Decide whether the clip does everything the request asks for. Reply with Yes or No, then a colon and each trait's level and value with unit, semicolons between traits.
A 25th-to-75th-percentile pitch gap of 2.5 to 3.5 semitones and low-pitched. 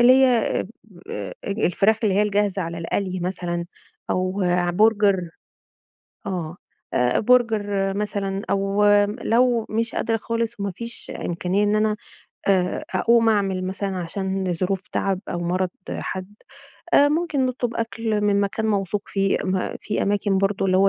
No: average, 2.8 semitones; high, 200 Hz